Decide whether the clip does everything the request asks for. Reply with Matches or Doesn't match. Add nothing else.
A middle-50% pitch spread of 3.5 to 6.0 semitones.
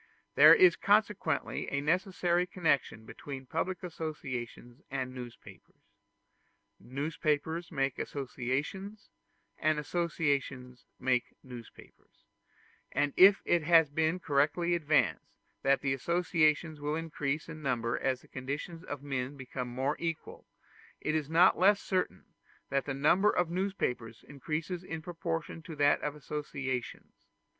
Matches